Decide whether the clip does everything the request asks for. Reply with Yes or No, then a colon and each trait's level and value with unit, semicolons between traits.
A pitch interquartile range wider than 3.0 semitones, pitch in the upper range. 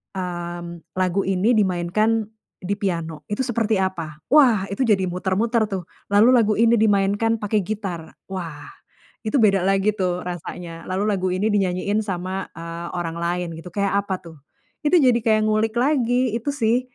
Yes: average, 3.7 semitones; high, 195 Hz